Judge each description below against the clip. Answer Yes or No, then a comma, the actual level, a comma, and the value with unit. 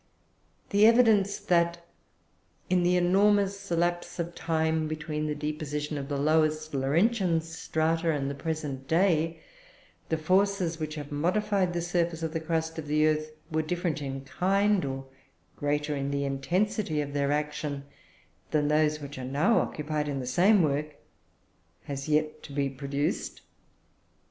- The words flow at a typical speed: Yes, average, 150 wpm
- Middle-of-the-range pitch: Yes, medium, 155 Hz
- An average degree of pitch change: Yes, average, 3.0 semitones